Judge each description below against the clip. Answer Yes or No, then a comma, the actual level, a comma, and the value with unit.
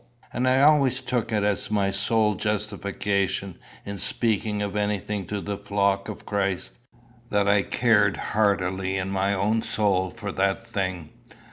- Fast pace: No, average, 150 wpm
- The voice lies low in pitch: Yes, low, 100 Hz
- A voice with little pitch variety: Yes, narrow, 1.7 semitones